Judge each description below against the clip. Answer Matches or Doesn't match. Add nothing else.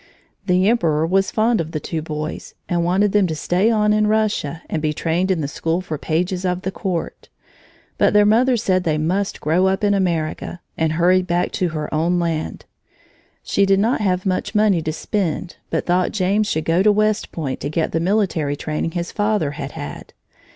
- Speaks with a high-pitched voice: Doesn't match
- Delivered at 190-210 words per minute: Matches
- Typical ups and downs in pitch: Matches